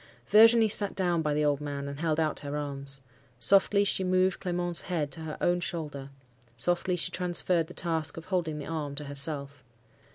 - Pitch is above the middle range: No, medium, 160 Hz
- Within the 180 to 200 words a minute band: Yes, average, 190 wpm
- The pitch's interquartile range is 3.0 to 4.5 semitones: Yes, average, 3.7 semitones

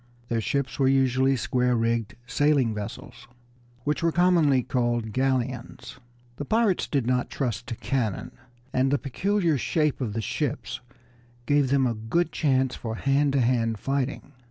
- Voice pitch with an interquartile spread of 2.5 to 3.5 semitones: Yes, average, 3.2 semitones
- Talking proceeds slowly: No, average, 155 wpm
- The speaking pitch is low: Yes, low, 130 Hz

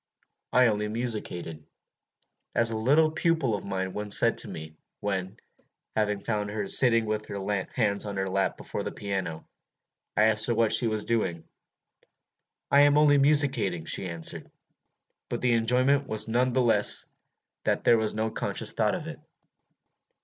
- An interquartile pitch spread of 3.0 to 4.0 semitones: Yes, average, 3.7 semitones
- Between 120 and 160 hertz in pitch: No, low, 110 Hz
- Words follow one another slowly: No, average, 165 wpm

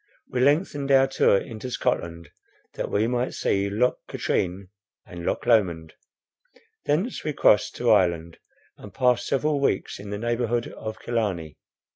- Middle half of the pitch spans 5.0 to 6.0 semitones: Yes, wide, 5.5 semitones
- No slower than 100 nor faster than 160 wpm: Yes, average, 145 wpm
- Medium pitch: No, low, 115 Hz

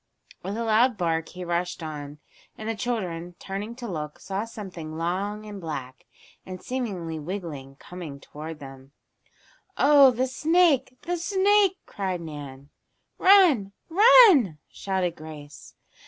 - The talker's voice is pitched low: No, high, 190 Hz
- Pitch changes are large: Yes, wide, 7.6 semitones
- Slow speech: Yes, slow, 130 wpm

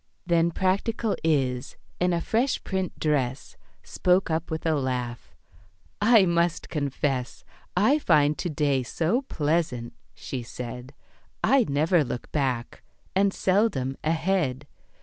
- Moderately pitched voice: Yes, medium, 160 Hz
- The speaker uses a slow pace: Yes, slow, 125 wpm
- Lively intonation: Yes, wide, 5.7 semitones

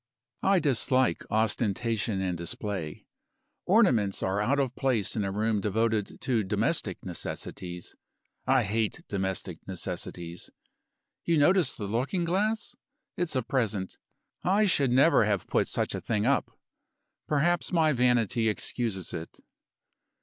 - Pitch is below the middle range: Yes, low, 115 Hz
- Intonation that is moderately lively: No, wide, 6.1 semitones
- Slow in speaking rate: Yes, slow, 130 wpm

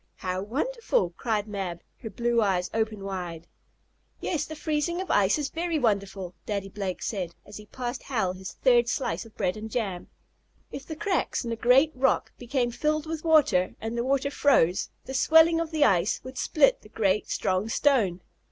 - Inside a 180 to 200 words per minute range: Yes, average, 185 wpm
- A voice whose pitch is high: Yes, high, 230 Hz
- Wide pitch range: Yes, wide, 6.7 semitones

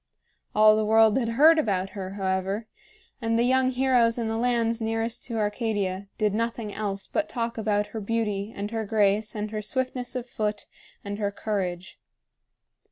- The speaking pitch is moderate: No, high, 220 Hz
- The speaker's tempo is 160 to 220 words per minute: Yes, average, 170 wpm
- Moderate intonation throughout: No, narrow, 2.2 semitones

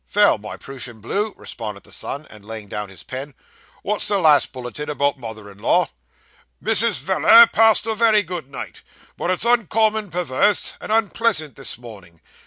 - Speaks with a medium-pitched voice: Yes, medium, 155 Hz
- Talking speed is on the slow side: No, average, 165 wpm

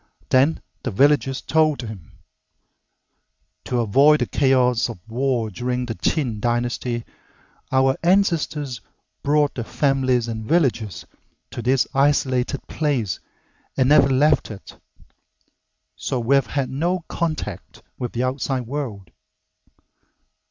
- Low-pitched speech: Yes, low, 130 Hz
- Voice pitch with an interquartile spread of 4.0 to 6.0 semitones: No, average, 3.4 semitones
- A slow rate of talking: Yes, slow, 115 wpm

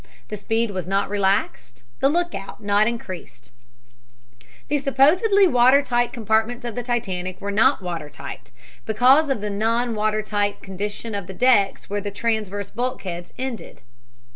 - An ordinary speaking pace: Yes, average, 155 wpm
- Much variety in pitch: No, average, 3.8 semitones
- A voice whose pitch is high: Yes, high, 215 Hz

